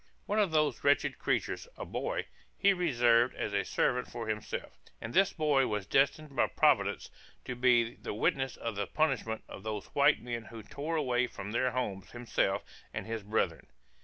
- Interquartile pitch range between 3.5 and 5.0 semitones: Yes, average, 4.3 semitones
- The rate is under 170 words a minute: No, average, 180 wpm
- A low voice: Yes, low, 120 Hz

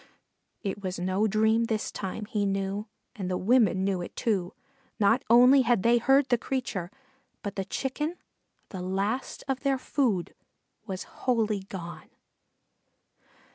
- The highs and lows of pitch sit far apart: No, average, 4.2 semitones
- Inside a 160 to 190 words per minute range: No, average, 140 wpm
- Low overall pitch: No, high, 210 Hz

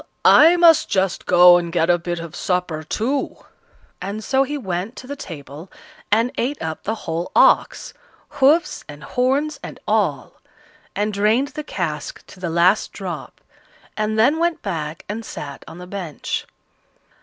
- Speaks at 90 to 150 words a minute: No, average, 160 wpm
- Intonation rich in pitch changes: Yes, wide, 7.2 semitones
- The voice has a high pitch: Yes, high, 195 Hz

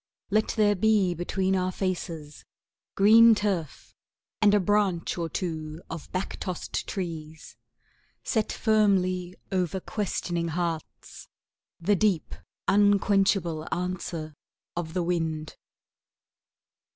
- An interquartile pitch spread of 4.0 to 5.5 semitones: No, average, 3.5 semitones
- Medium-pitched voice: Yes, medium, 180 Hz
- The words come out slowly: Yes, slow, 105 wpm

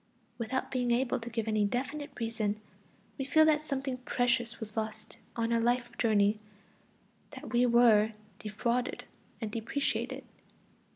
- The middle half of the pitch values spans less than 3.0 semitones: Yes, narrow, 2.4 semitones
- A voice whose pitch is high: Yes, high, 235 Hz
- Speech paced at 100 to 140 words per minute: Yes, slow, 135 wpm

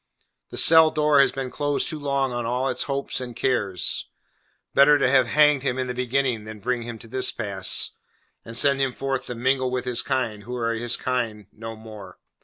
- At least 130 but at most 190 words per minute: No, fast, 205 wpm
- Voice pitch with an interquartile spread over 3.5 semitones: No, average, 2.9 semitones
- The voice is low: Yes, low, 125 Hz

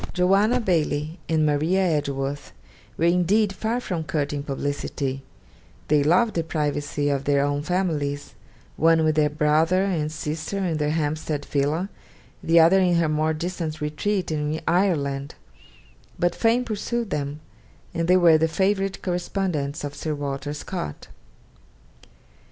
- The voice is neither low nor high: Yes, medium, 155 Hz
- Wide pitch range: No, average, 3.7 semitones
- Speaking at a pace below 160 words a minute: Yes, average, 140 wpm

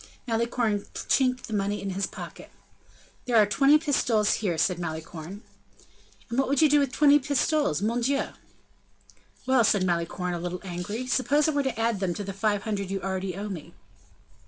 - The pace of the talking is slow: No, average, 180 wpm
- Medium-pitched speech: No, high, 210 Hz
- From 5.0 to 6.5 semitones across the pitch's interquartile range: Yes, wide, 5.5 semitones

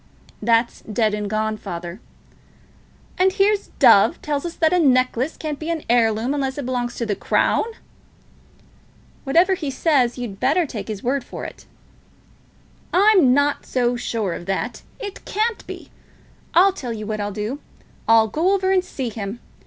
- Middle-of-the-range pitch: No, very high, 255 Hz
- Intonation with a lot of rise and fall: Yes, wide, 6.8 semitones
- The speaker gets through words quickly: No, average, 165 wpm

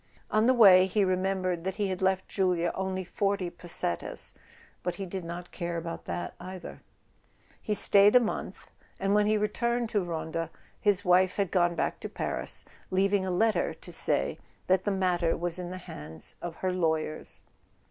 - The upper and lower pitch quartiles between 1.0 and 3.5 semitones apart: Yes, narrow, 2.4 semitones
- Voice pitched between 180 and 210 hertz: Yes, medium, 185 Hz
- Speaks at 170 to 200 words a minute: Yes, average, 180 wpm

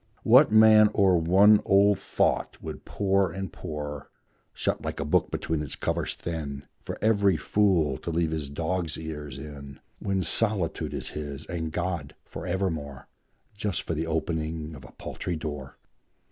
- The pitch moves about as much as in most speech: Yes, average, 4.4 semitones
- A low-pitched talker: Yes, very low, 80 Hz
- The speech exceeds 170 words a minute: No, average, 160 wpm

